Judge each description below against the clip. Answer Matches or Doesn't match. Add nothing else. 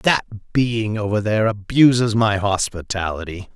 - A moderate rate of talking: Doesn't match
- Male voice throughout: Matches